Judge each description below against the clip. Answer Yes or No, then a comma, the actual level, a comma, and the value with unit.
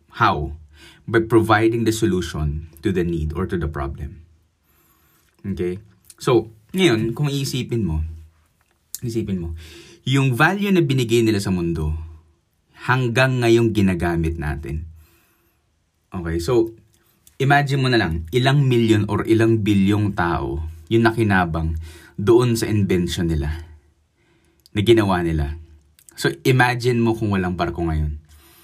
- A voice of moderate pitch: No, very low, 90 Hz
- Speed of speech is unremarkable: Yes, average, 125 wpm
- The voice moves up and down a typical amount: No, wide, 5.9 semitones